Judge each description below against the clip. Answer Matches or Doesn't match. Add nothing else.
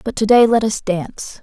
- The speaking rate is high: Matches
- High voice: Matches